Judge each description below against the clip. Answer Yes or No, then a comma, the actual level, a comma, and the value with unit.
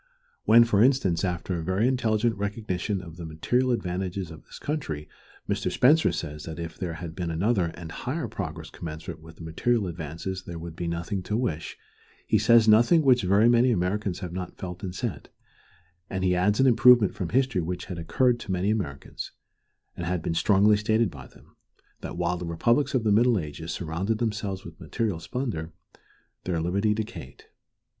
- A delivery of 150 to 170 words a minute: No, average, 185 wpm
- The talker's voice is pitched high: No, very low, 95 Hz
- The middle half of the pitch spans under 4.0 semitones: No, average, 5.1 semitones